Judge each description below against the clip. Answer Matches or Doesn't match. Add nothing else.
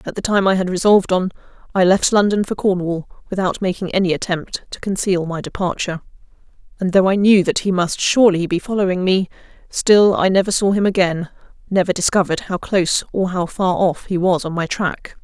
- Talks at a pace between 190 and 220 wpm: Matches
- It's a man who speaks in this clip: Doesn't match